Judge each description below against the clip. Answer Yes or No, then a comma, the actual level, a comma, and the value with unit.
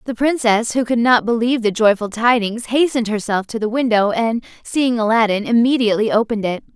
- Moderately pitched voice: No, high, 230 Hz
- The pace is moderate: Yes, average, 180 wpm